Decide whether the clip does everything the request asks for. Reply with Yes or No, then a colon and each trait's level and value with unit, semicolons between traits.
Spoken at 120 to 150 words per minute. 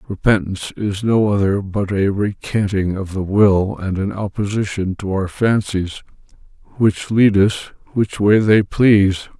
Yes: average, 145 wpm